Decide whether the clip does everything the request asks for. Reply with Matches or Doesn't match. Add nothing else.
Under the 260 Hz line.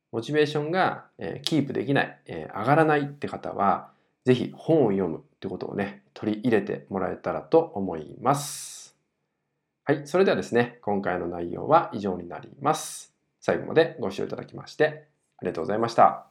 Matches